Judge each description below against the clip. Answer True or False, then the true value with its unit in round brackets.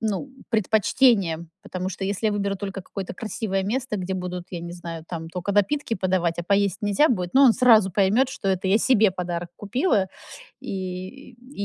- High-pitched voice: True (195 Hz)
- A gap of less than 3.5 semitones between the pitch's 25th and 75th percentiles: True (3.1 semitones)